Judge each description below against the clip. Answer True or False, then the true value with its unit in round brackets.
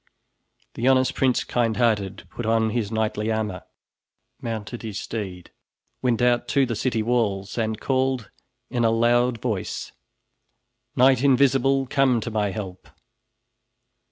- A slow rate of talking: True (130 wpm)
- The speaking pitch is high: False (115 Hz)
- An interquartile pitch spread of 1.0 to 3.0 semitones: True (2.7 semitones)